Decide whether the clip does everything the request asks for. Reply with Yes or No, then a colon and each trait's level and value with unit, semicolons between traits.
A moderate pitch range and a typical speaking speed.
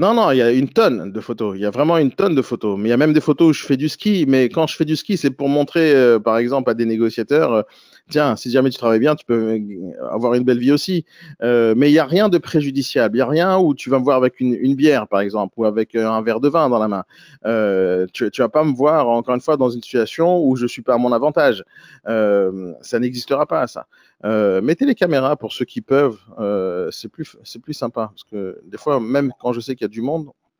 No: average, 4.8 semitones; fast, 280 wpm